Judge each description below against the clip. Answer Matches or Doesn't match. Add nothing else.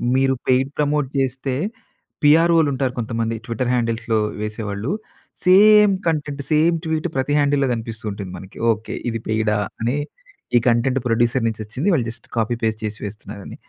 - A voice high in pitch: Doesn't match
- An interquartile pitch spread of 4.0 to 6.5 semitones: Matches